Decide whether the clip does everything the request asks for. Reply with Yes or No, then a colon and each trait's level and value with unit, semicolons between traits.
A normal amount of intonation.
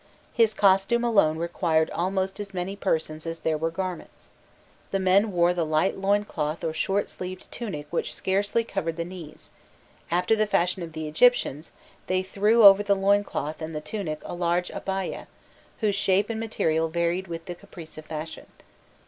Yes: average, 3.5 semitones